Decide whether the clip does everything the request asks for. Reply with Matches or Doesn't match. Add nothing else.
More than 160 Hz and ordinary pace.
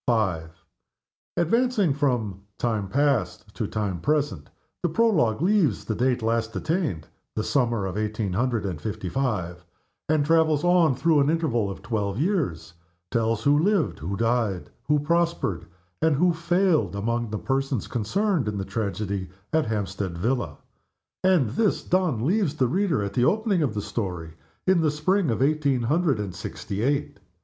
Doesn't match